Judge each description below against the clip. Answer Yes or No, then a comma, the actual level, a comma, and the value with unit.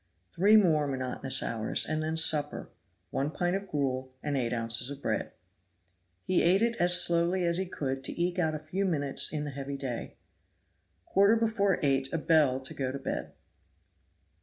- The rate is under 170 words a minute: No, average, 180 wpm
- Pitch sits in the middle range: Yes, medium, 155 Hz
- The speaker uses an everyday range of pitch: Yes, average, 4.8 semitones